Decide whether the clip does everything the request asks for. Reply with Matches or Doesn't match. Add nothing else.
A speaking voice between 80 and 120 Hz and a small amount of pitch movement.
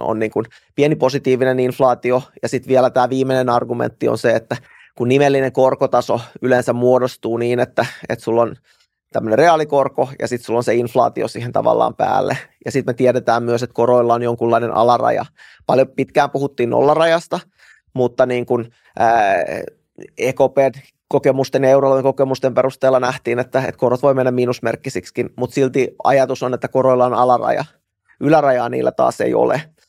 Doesn't match